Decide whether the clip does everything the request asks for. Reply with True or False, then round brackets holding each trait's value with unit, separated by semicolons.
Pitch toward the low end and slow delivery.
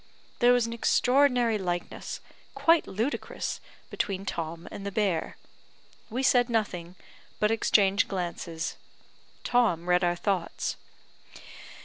False (200 Hz; 110 wpm)